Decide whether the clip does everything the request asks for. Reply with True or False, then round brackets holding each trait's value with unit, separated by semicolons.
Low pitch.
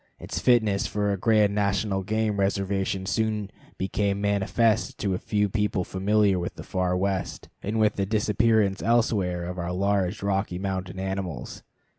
True (100 Hz)